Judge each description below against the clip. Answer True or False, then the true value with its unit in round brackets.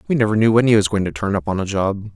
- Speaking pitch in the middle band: False (105 Hz)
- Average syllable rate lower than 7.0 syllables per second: False (7.1 syllables/s)